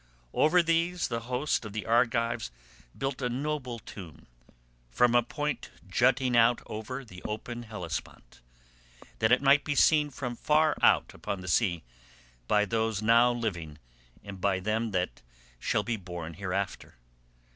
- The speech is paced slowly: No, average, 145 wpm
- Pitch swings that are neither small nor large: Yes, average, 4.4 semitones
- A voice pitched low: Yes, low, 115 Hz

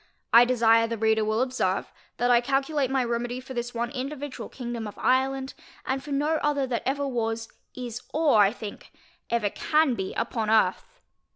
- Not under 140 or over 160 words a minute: No, average, 180 wpm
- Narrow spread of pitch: No, average, 3.0 semitones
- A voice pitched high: Yes, high, 245 Hz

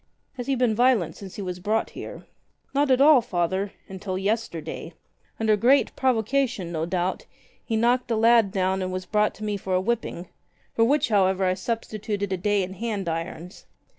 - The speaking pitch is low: No, high, 205 Hz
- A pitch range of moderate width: Yes, average, 3.9 semitones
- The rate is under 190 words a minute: No, average, 195 wpm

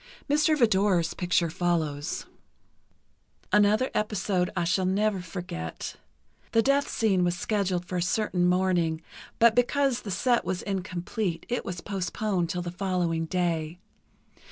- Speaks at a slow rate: Yes, slow, 130 wpm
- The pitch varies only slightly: No, average, 3.4 semitones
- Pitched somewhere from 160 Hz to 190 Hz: Yes, medium, 185 Hz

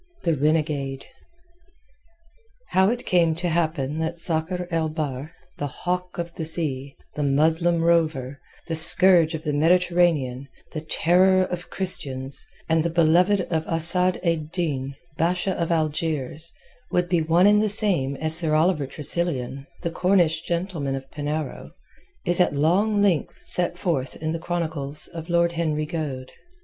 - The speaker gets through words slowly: No, average, 150 wpm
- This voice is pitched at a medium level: Yes, medium, 165 Hz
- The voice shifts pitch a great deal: No, average, 2.8 semitones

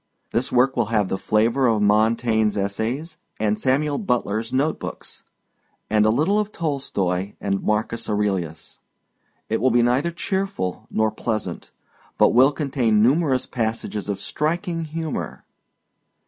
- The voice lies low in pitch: Yes, low, 115 Hz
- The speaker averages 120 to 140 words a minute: Yes, slow, 135 wpm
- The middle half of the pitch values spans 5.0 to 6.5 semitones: Yes, average, 5.3 semitones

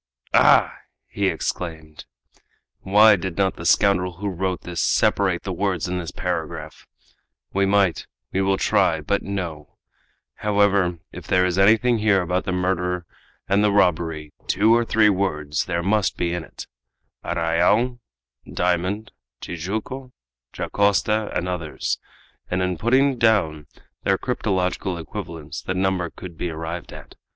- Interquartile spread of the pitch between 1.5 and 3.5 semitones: Yes, average, 3.0 semitones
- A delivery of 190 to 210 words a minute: No, average, 140 wpm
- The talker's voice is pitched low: Yes, very low, 95 Hz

